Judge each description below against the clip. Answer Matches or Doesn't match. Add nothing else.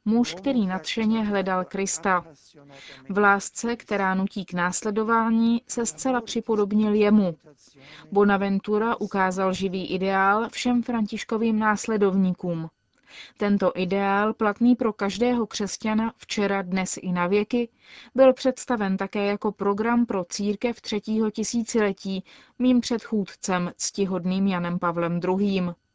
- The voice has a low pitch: Doesn't match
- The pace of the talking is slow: Matches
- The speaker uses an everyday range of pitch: Matches